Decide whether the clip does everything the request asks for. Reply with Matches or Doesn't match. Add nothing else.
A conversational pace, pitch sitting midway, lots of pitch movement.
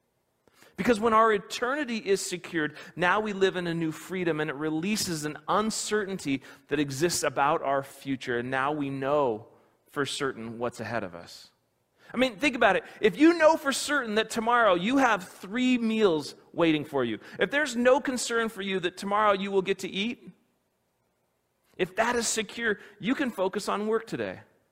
Doesn't match